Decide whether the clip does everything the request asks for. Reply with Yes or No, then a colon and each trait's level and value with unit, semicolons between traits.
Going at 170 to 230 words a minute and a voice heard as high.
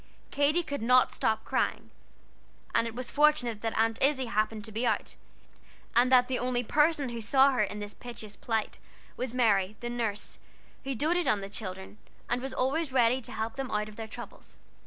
Yes: average, 195 wpm; high, 240 Hz